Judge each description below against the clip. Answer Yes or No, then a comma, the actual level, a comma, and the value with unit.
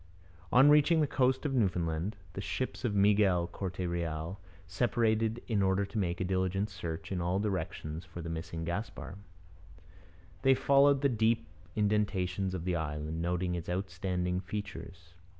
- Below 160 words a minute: Yes, average, 150 wpm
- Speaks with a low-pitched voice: Yes, very low, 95 Hz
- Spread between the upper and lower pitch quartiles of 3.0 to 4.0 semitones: Yes, average, 3.7 semitones